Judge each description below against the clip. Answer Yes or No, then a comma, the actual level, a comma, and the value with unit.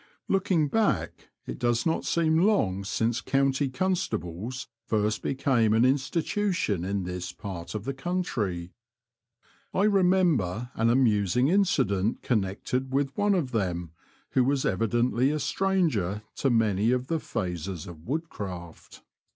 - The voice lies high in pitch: No, low, 125 Hz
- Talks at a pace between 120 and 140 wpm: Yes, slow, 135 wpm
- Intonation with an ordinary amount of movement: No, wide, 7.7 semitones